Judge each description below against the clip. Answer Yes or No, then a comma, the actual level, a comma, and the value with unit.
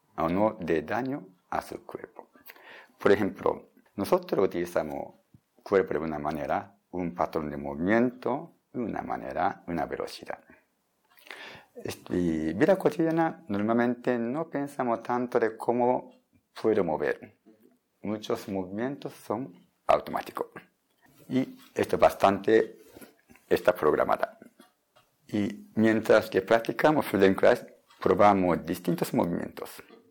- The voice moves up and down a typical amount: No, wide, 6.7 semitones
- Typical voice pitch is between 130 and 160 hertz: No, low, 115 Hz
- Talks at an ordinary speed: No, slow, 110 wpm